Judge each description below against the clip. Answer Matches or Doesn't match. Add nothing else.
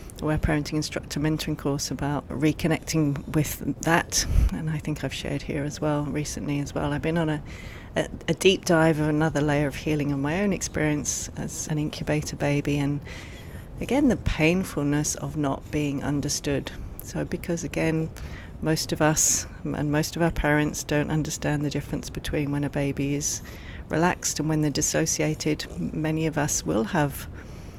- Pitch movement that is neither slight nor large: Doesn't match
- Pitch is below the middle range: Doesn't match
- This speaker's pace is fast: Doesn't match